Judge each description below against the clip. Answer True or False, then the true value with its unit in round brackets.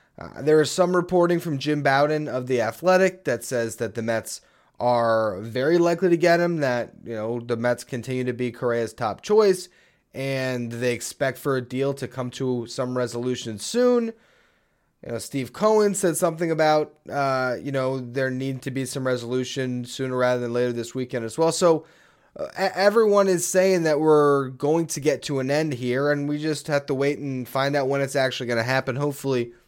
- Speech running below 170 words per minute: False (200 wpm)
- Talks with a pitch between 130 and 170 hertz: True (135 Hz)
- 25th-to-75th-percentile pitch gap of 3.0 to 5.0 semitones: True (4.1 semitones)